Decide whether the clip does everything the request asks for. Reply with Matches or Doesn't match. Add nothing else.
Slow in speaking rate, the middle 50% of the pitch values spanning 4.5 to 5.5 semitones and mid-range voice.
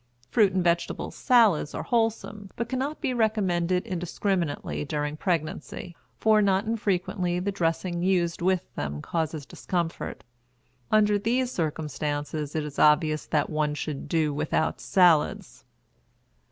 Matches